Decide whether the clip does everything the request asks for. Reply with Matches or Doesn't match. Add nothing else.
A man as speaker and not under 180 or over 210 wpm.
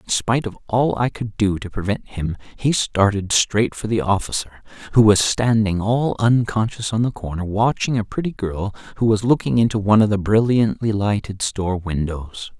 Matches